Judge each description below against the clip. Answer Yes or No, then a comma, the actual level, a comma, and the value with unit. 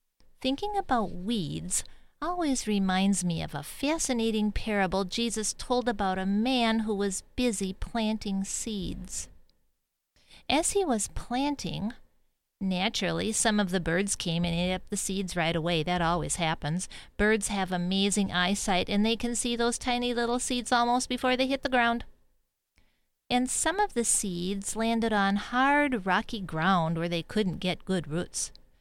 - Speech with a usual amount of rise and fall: Yes, average, 4.6 semitones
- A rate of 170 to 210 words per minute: No, average, 155 wpm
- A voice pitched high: Yes, high, 210 Hz